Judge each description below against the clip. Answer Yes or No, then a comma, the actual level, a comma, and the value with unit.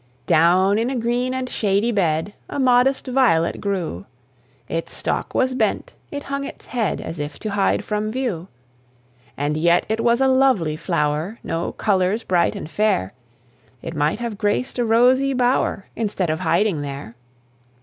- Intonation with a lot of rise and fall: Yes, wide, 6.9 semitones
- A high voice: Yes, high, 210 Hz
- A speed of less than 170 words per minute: Yes, average, 160 wpm